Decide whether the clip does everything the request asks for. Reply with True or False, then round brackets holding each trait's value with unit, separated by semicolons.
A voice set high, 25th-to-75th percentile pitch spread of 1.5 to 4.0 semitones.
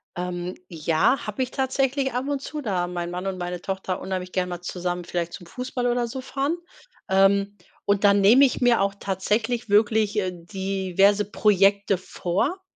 False (200 Hz; 4.9 semitones)